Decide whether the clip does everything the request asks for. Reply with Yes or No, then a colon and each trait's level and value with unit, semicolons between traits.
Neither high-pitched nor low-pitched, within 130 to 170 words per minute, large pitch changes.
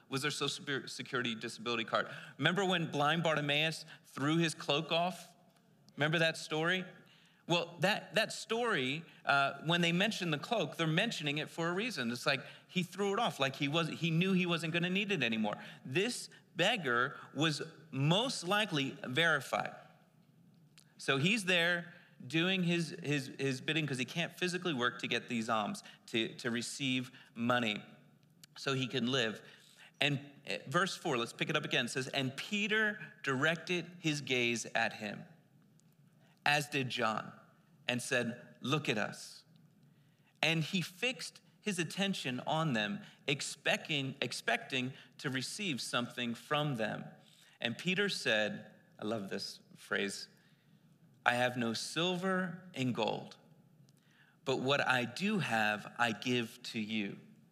No: medium, 160 Hz; average, 150 wpm; average, 5.0 semitones